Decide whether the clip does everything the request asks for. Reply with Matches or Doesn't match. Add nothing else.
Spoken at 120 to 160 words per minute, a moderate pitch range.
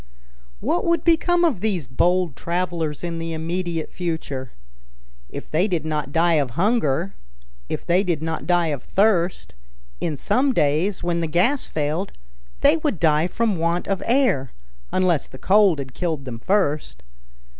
Matches